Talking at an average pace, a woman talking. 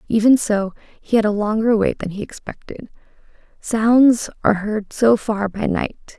Yes: average, 165 wpm; female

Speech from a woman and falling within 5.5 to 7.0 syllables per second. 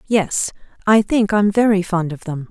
No: female; 4.5 syllables/s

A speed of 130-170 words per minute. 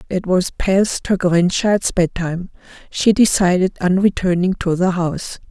Yes: average, 140 wpm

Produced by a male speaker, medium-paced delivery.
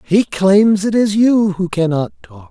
Yes: male; average, 190 wpm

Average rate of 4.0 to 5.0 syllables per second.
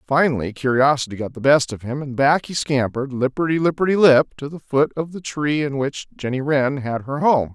No: 5.5 syllables/s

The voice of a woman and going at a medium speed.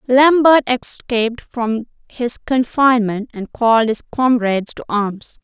No: female; slow, 120 wpm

